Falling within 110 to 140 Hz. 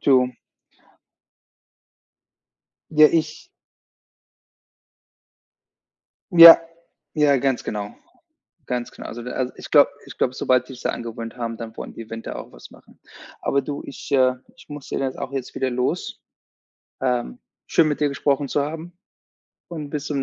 Yes: low, 135 Hz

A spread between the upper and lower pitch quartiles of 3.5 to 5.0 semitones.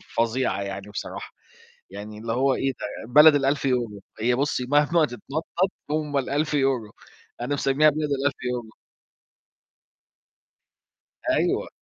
Yes: average, 4.0 semitones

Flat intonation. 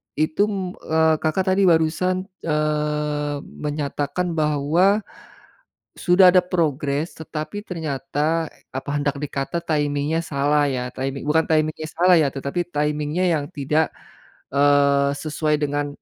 Yes: narrow, 2.3 semitones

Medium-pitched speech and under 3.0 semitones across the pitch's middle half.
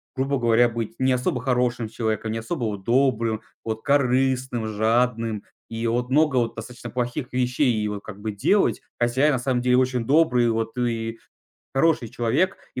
No: low, 120 Hz; narrow, 2.4 semitones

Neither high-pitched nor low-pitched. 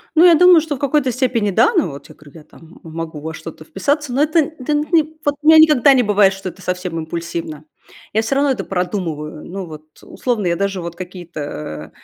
No: high, 195 Hz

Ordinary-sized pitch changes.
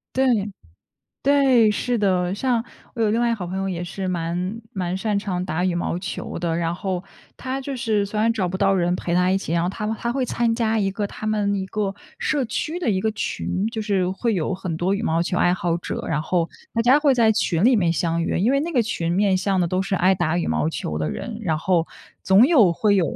Yes: average, 4.2 semitones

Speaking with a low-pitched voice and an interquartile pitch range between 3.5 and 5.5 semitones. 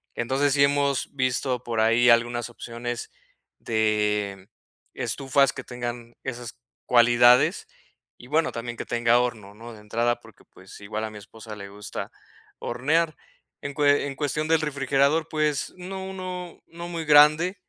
Yes: low, 125 Hz; average, 4.0 semitones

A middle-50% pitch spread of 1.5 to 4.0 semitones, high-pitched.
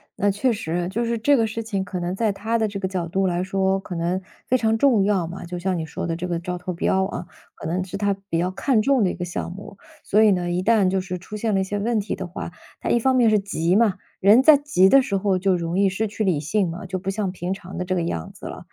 Yes: average, 3.1 semitones; high, 195 Hz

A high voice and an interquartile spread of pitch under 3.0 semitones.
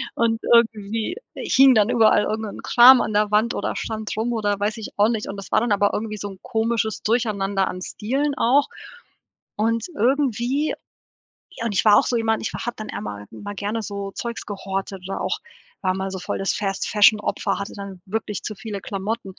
Yes: high, 215 Hz; narrow, 2.4 semitones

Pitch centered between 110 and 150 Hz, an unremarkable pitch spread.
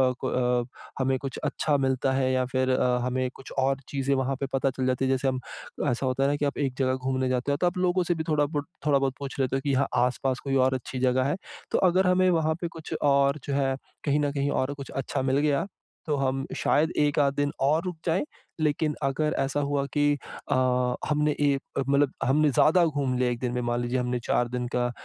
No: low, 135 Hz; narrow, 2.1 semitones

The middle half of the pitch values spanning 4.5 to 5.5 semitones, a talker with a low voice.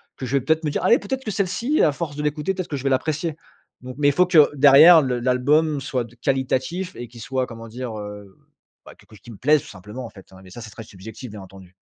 Yes: average, 5.1 semitones; low, 130 Hz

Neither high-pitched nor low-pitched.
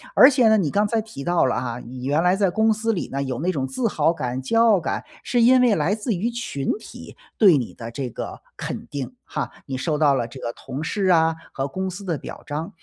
Yes: medium, 165 Hz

